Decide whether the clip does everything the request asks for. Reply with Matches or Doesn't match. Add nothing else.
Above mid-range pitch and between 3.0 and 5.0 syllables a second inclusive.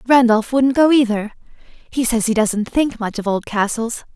Matches